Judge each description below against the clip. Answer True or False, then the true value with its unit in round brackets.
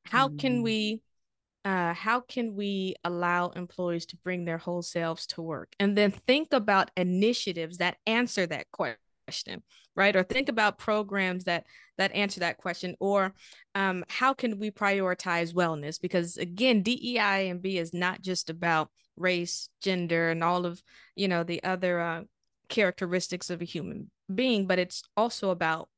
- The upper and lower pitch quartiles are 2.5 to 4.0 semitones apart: True (2.9 semitones)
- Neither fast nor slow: True (160 wpm)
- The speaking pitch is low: False (185 Hz)